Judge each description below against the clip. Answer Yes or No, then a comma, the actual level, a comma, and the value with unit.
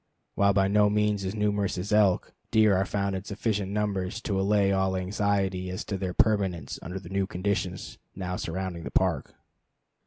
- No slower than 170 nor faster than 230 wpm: Yes, average, 180 wpm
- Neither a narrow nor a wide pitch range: No, narrow, 1.7 semitones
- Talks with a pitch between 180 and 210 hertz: No, low, 100 Hz